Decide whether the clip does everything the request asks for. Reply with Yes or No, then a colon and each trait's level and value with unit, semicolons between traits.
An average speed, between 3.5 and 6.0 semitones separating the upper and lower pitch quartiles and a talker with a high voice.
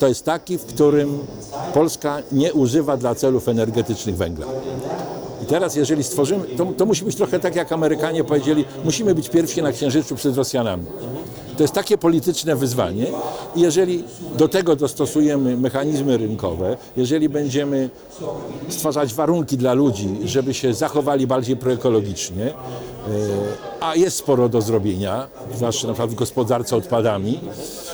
No: average, 140 wpm; average, 4.2 semitones; medium, 140 Hz